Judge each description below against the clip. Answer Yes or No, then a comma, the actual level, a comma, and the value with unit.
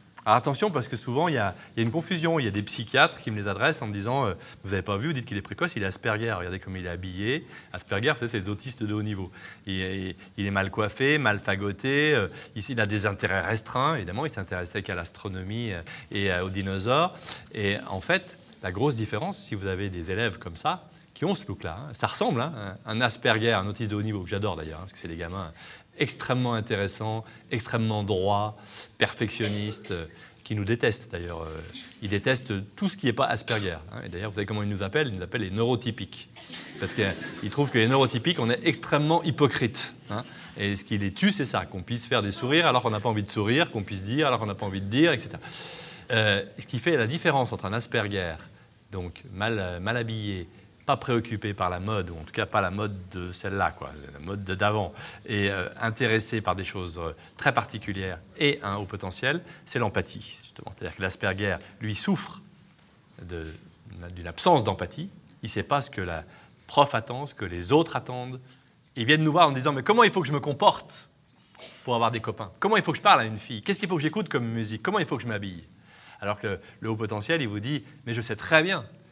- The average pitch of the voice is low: Yes, low, 110 Hz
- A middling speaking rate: No, fast, 235 wpm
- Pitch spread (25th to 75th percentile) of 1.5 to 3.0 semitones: No, average, 5.2 semitones